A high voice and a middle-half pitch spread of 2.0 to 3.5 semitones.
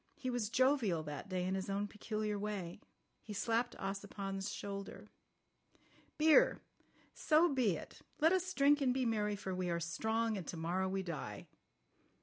No: high, 205 Hz; average, 4.7 semitones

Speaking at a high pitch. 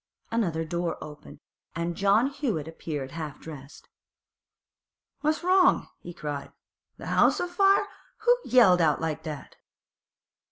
No: medium, 170 Hz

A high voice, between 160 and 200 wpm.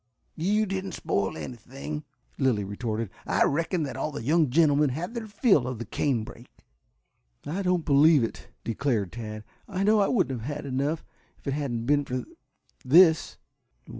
No: medium, 145 Hz; average, 165 wpm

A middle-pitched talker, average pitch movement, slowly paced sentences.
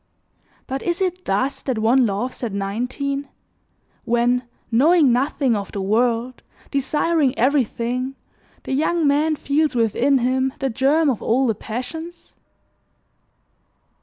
No: very high, 260 Hz; average, 3.3 semitones; slow, 125 wpm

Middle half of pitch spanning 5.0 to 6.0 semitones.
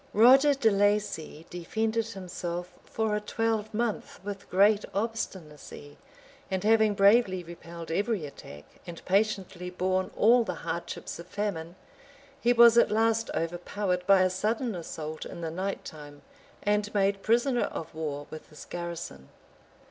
No: average, 4.3 semitones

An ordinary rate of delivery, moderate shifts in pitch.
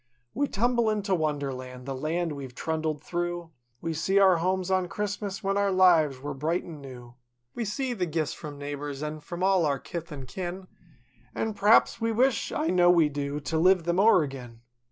Yes: average, 185 wpm; average, 4.9 semitones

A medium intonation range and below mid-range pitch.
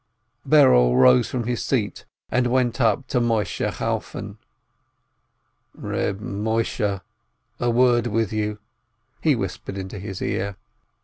Yes: average, 3.7 semitones; low, 110 Hz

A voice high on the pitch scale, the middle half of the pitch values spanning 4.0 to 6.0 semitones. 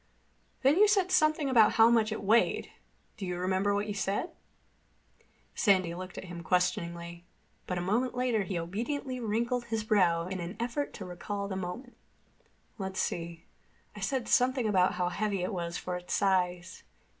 Yes: high, 200 Hz; average, 4.8 semitones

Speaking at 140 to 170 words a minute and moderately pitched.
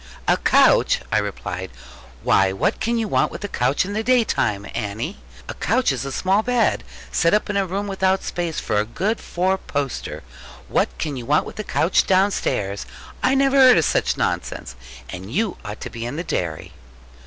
No: average, 200 wpm; medium, 175 Hz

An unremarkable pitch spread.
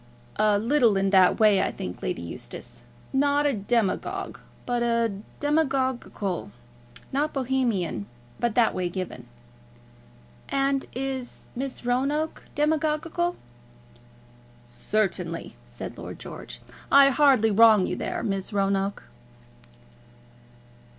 No: wide, 5.9 semitones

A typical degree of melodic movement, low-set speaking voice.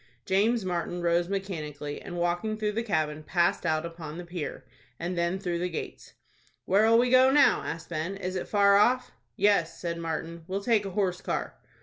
No: average, 3.3 semitones; medium, 180 Hz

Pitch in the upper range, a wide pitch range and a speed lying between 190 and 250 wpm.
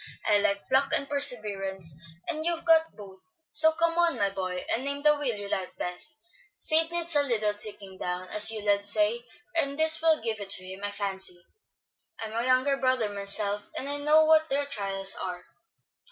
Yes: high, 225 Hz; wide, 6.6 semitones; average, 195 wpm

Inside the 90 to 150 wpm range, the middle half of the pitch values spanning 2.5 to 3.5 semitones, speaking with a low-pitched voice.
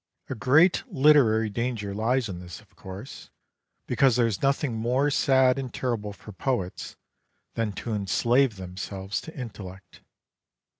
No: average, 140 wpm; average, 4.7 semitones; low, 115 Hz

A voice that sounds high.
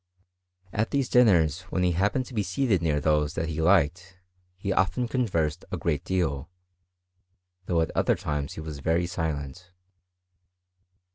No: very low, 85 Hz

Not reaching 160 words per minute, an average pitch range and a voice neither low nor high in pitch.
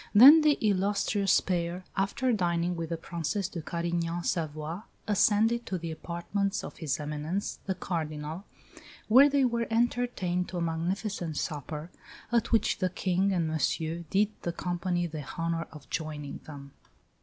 Yes: average, 150 wpm; average, 3.7 semitones; medium, 175 Hz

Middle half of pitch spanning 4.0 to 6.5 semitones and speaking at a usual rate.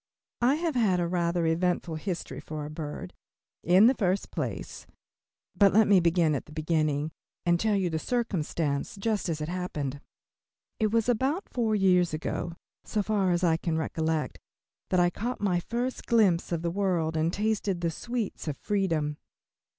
Yes: average, 4.6 semitones; average, 175 wpm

